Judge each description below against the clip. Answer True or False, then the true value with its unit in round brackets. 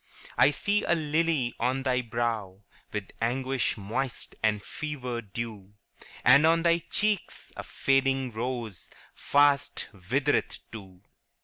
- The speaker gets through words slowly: True (125 wpm)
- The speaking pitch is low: True (125 Hz)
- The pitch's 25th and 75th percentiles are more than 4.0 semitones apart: True (4.5 semitones)